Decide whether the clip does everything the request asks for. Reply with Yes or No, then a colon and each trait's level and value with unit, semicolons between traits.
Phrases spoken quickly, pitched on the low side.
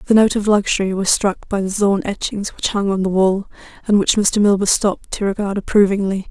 No: fast, 220 wpm; high, 200 Hz